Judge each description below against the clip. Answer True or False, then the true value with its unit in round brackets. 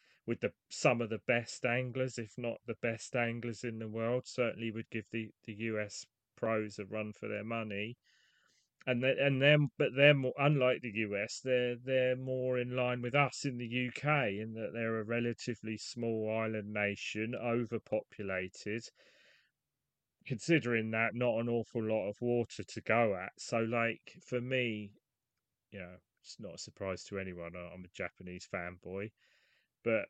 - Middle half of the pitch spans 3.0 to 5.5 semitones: False (2.5 semitones)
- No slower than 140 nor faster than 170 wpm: True (165 wpm)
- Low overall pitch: True (115 Hz)